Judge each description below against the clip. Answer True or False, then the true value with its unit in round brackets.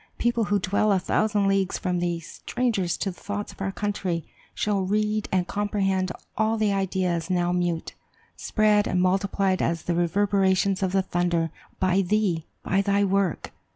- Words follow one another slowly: False (165 wpm)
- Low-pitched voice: False (195 Hz)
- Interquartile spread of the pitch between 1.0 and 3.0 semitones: True (2.4 semitones)